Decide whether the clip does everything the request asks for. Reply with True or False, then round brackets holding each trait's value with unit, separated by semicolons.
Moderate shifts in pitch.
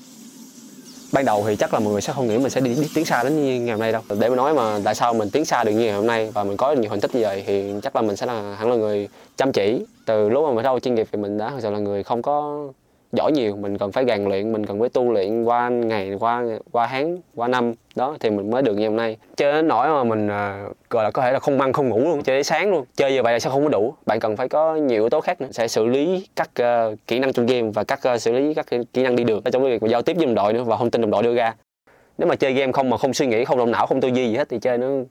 True (4.0 semitones)